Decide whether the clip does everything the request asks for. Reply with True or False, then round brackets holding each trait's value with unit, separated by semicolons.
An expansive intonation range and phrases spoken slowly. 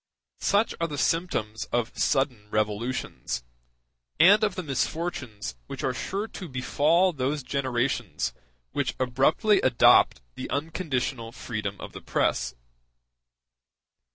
True (6.5 semitones; 115 wpm)